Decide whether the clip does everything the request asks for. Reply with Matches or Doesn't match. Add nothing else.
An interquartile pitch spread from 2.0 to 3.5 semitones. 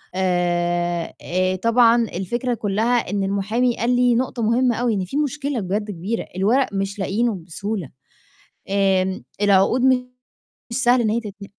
Doesn't match